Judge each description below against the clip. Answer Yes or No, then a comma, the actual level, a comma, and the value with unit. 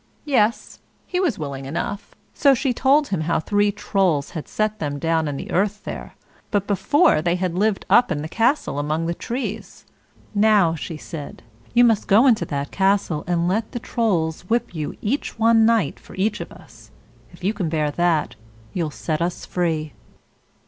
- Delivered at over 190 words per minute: No, average, 185 wpm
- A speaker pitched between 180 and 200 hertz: Yes, high, 190 Hz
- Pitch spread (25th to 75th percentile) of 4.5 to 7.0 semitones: Yes, wide, 5.5 semitones